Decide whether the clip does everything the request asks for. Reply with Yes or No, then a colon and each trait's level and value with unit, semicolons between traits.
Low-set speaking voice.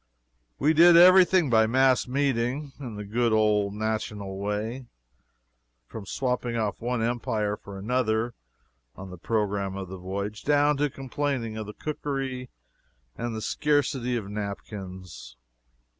Yes: low, 115 Hz